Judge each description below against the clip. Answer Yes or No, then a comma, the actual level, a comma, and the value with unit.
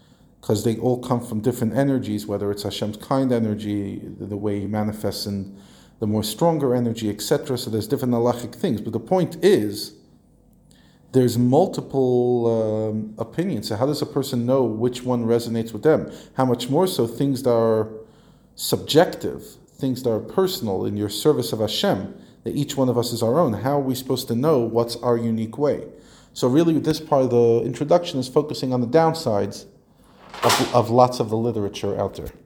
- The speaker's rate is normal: Yes, average, 185 wpm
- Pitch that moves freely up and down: No, average, 3.3 semitones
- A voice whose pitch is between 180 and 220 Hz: No, low, 120 Hz